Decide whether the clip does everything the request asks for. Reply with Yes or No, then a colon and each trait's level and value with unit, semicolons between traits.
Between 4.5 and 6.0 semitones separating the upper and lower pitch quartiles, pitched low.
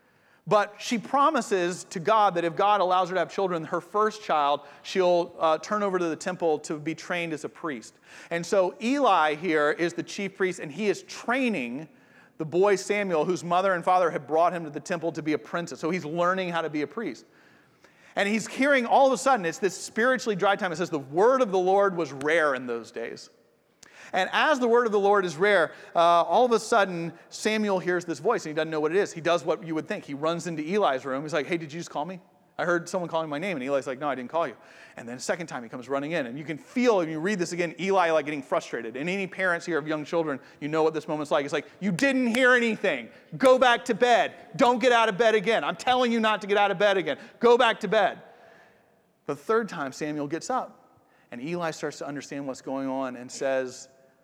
No: average, 4.9 semitones; medium, 180 Hz